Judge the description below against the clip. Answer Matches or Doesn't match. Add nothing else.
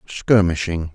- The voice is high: Doesn't match